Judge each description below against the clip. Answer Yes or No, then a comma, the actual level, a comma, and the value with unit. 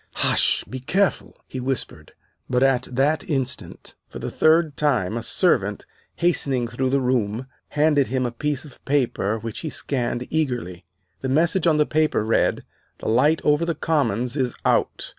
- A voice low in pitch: Yes, low, 130 Hz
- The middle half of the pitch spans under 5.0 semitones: Yes, average, 3.8 semitones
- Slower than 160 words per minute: No, average, 165 wpm